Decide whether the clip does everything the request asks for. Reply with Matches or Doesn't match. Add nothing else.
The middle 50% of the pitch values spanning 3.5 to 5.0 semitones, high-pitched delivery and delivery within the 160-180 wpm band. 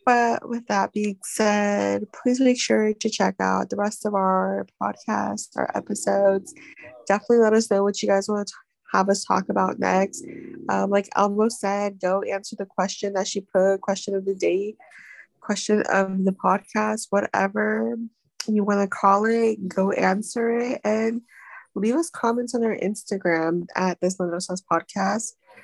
Doesn't match